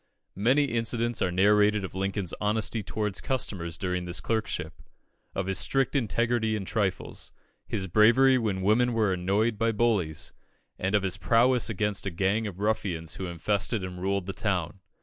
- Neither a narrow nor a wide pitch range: Yes, average, 3.2 semitones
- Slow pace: No, average, 165 wpm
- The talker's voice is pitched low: Yes, low, 105 Hz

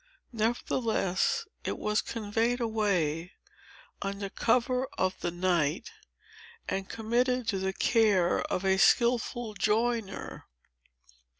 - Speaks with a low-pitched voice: No, high, 215 Hz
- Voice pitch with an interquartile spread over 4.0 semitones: No, average, 3.7 semitones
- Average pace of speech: No, slow, 100 wpm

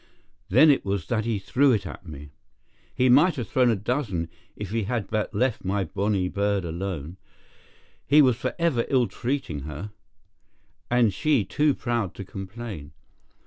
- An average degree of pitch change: Yes, average, 4.8 semitones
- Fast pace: No, average, 160 wpm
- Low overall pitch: Yes, low, 105 Hz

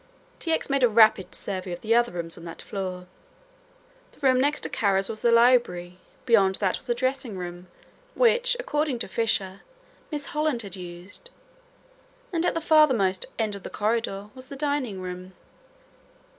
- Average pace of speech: Yes, average, 170 wpm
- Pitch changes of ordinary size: No, wide, 6.3 semitones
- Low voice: No, high, 225 Hz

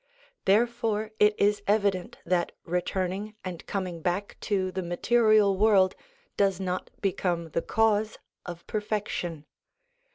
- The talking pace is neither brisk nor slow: No, slow, 120 wpm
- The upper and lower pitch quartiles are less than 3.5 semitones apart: Yes, average, 2.8 semitones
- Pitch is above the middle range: Yes, high, 195 Hz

